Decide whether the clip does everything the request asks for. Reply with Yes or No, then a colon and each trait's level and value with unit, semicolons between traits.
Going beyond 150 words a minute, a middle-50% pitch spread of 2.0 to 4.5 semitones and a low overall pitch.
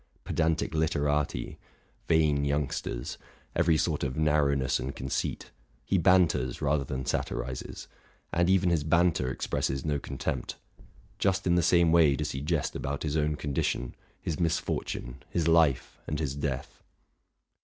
No: average, 145 wpm; average, 3.4 semitones; very low, 75 Hz